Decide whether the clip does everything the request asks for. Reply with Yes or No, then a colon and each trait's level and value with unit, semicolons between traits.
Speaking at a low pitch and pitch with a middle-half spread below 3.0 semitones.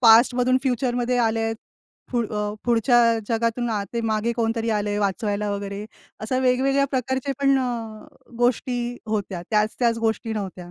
No: high, 230 Hz; narrow, 2.4 semitones